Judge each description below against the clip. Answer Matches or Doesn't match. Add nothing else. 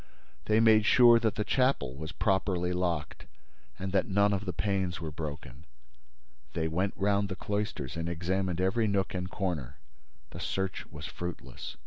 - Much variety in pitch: Doesn't match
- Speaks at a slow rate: Doesn't match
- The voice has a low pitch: Matches